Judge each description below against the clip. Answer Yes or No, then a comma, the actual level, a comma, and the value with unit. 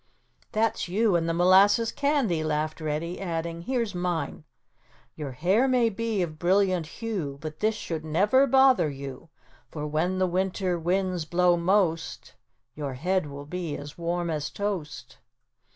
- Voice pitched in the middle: Yes, medium, 175 Hz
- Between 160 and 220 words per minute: No, average, 150 wpm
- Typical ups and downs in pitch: Yes, average, 4.3 semitones